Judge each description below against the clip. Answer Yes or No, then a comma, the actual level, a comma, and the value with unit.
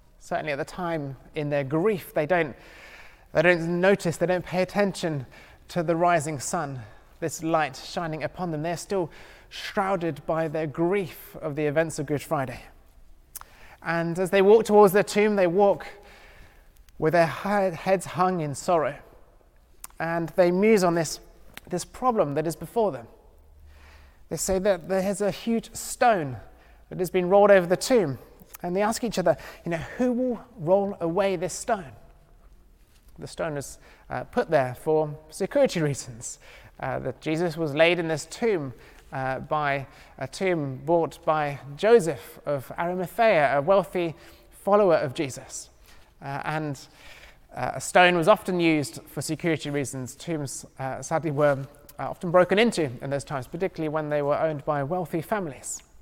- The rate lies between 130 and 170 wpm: Yes, average, 160 wpm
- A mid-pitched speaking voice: Yes, medium, 165 Hz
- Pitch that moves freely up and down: No, average, 4.5 semitones